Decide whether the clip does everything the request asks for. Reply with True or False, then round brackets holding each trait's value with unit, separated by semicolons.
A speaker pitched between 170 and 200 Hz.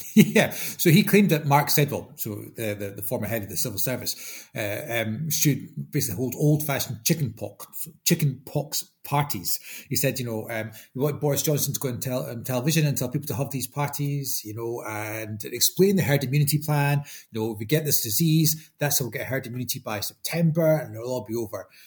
False (135 Hz)